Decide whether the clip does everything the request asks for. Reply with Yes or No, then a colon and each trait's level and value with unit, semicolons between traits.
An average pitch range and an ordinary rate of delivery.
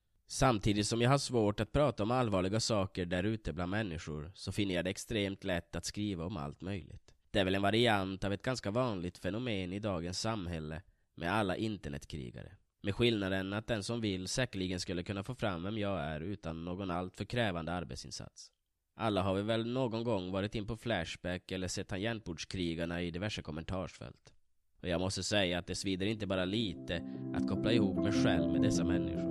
Yes: average, 4.0 semitones; average, 190 wpm